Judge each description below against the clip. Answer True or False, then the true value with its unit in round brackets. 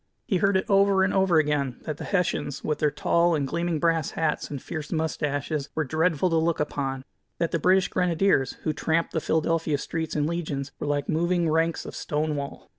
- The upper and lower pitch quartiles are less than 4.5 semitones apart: True (2.5 semitones)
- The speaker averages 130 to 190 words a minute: False (200 wpm)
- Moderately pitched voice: True (160 Hz)